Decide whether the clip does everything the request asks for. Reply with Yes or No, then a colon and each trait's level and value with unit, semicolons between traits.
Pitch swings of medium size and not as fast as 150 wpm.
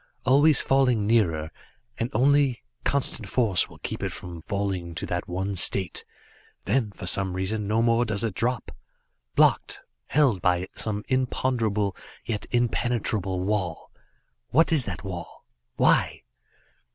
Yes: average, 4.6 semitones; slow, 135 wpm